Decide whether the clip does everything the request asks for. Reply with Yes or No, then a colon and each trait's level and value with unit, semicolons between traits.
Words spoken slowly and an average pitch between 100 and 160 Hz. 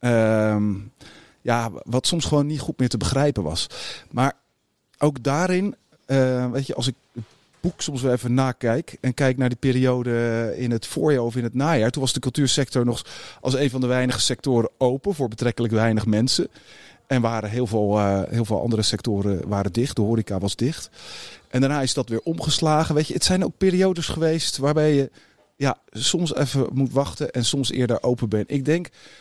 No: average, 195 wpm; low, 125 Hz